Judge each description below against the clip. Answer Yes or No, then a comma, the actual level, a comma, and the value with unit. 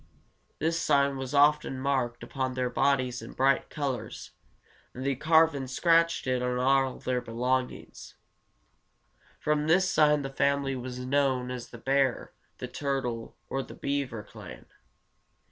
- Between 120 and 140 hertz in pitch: Yes, low, 135 Hz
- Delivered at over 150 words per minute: No, average, 145 wpm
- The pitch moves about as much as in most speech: No, narrow, 2.0 semitones